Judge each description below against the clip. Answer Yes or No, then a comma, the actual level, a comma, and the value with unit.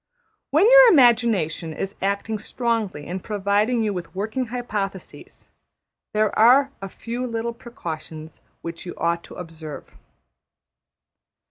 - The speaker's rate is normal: No, slow, 120 wpm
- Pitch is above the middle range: Yes, high, 210 Hz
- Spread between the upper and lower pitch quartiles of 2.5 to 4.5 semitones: No, average, 5.2 semitones